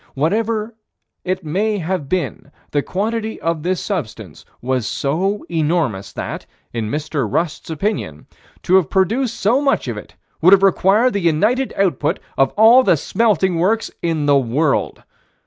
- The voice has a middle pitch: Yes, medium, 175 Hz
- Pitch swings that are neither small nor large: No, wide, 6.4 semitones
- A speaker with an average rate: Yes, average, 150 wpm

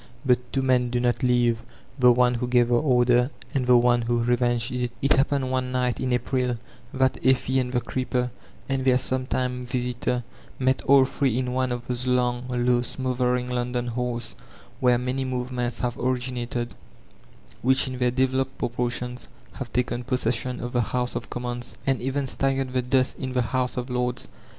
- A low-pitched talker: Yes, low, 125 Hz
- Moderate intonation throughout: No, narrow, 1.0 semitones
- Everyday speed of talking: Yes, average, 185 wpm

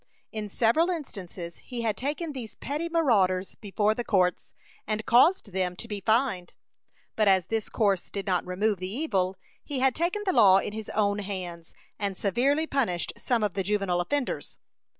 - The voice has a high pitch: Yes, high, 210 Hz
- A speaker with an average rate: Yes, average, 175 wpm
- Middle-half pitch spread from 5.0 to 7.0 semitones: Yes, average, 5.3 semitones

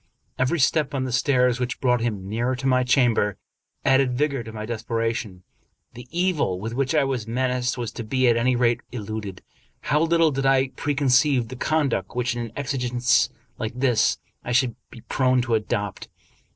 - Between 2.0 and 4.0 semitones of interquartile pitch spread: Yes, average, 2.7 semitones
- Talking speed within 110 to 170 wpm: No, average, 180 wpm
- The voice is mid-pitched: No, low, 125 Hz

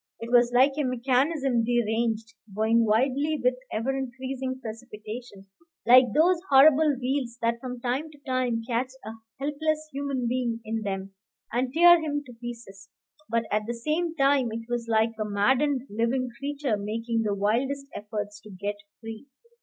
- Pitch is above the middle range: Yes, high, 245 Hz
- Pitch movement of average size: Yes, average, 3.3 semitones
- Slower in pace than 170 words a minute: Yes, average, 160 wpm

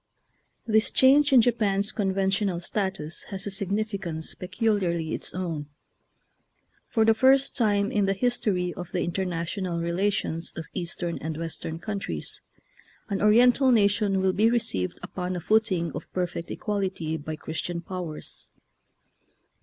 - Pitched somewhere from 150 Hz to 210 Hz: Yes, high, 190 Hz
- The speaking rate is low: Yes, slow, 130 wpm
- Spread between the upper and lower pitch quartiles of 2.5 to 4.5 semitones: Yes, average, 3.8 semitones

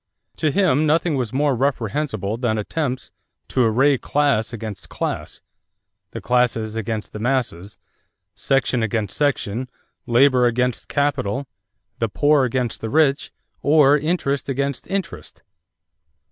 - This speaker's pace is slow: Yes, slow, 120 wpm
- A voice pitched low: Yes, low, 130 Hz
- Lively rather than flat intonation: No, average, 4.2 semitones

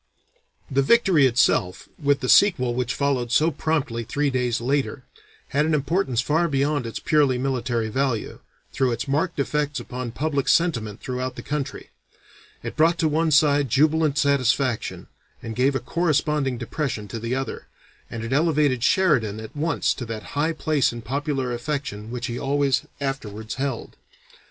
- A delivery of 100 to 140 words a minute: No, average, 160 wpm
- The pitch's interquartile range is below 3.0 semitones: No, average, 3.5 semitones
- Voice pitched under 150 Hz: Yes, low, 135 Hz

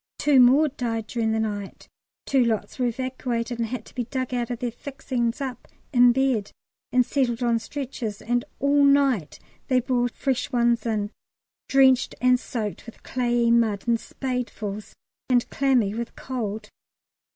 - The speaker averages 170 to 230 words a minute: No, average, 160 wpm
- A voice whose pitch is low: No, high, 245 Hz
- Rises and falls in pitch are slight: Yes, narrow, 2.2 semitones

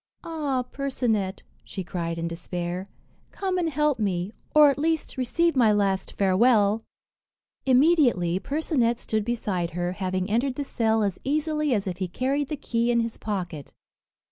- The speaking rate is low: No, average, 155 wpm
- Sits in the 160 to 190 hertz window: No, high, 230 Hz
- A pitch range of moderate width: No, wide, 6.9 semitones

